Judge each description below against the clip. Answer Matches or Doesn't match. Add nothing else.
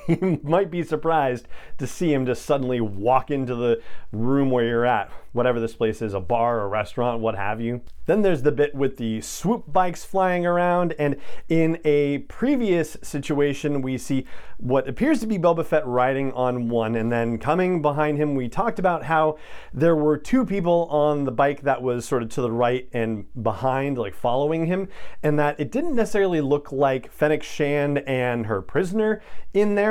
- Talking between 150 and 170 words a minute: Doesn't match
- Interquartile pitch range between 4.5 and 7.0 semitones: Matches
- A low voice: Doesn't match